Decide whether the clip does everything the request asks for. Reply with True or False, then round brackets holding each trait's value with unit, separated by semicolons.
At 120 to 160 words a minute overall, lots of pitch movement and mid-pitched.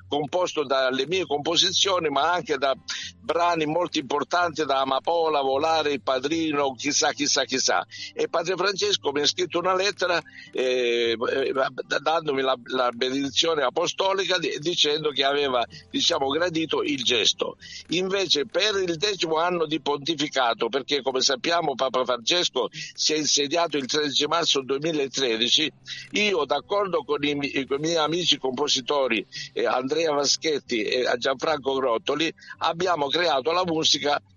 False (140 wpm; 4.2 semitones; 150 Hz)